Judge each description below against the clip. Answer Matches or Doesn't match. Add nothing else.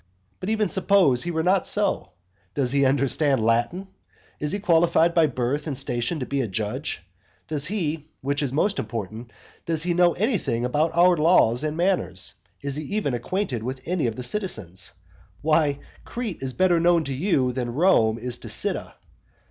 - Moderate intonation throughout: Doesn't match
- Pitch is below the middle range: Doesn't match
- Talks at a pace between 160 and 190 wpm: Matches